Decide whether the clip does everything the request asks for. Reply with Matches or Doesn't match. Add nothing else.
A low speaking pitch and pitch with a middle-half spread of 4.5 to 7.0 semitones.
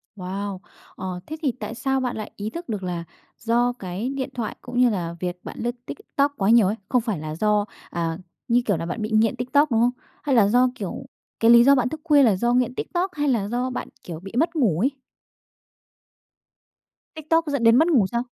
Doesn't match